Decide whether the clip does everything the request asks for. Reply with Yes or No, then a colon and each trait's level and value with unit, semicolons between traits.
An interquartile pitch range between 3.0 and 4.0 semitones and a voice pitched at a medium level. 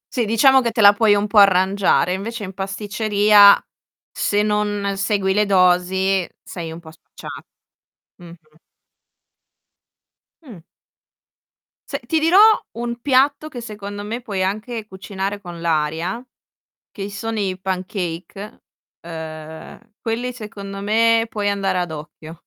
No: average, 3.3 semitones; high, 200 Hz